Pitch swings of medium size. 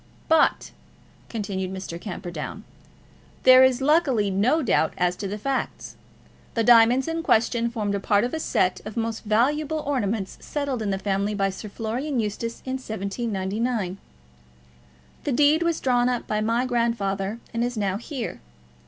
Yes: average, 4.3 semitones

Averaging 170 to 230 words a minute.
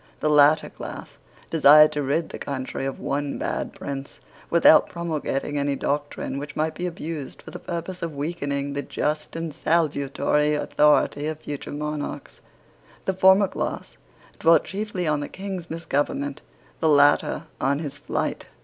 No: average, 150 wpm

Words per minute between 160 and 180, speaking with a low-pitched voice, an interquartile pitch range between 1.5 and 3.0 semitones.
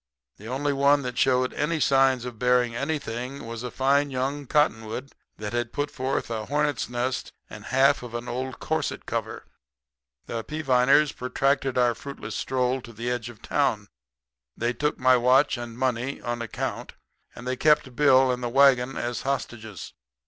Yes: average, 170 wpm; low, 130 Hz; narrow, 2.5 semitones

